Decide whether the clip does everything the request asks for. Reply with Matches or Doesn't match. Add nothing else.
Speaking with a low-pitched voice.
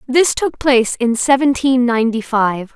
Doesn't match